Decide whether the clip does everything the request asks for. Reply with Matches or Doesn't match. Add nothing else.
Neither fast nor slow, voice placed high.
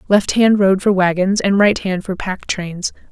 Matches